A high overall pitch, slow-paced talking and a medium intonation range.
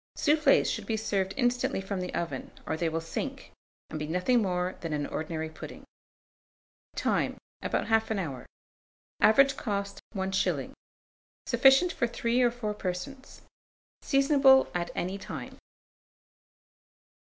No: high, 200 Hz; slow, 130 wpm; wide, 5.7 semitones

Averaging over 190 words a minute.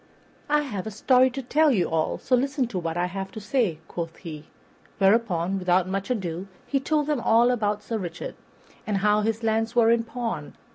Yes: average, 200 wpm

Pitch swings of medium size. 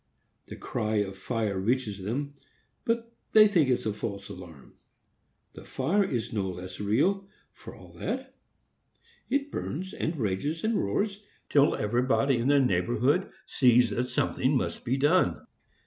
No: wide, 7.5 semitones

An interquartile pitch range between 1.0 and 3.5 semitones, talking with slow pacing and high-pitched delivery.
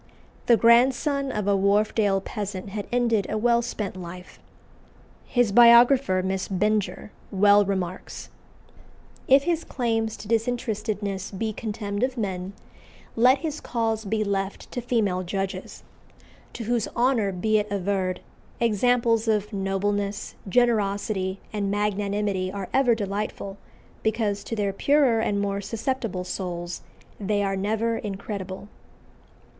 Yes: average, 2.9 semitones; slow, 125 wpm; high, 210 Hz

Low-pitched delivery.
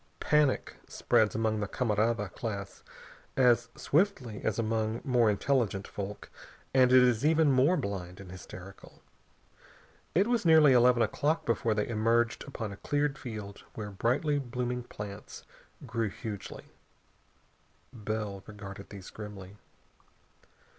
Yes: low, 115 Hz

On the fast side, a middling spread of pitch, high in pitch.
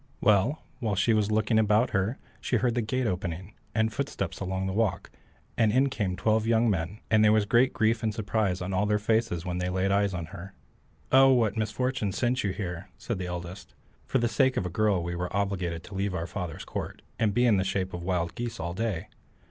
No: fast, 225 wpm; average, 3.4 semitones; low, 105 Hz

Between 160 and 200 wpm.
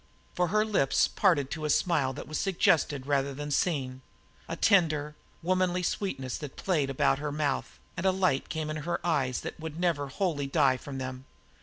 Yes: average, 185 wpm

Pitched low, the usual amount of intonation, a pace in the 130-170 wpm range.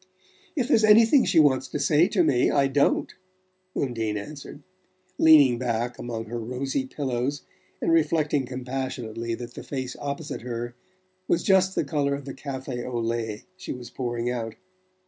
Yes: low, 130 Hz; average, 3.6 semitones; average, 160 wpm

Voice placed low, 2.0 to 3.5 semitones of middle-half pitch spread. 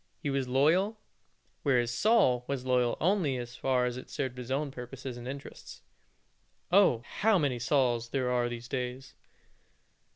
Yes: low, 130 Hz; narrow, 2.5 semitones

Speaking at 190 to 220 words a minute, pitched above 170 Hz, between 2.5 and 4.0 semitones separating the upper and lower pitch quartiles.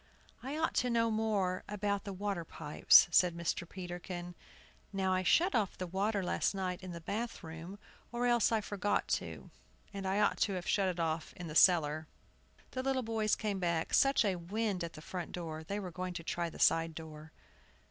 Yes: average, 200 wpm; medium, 185 Hz; average, 3.5 semitones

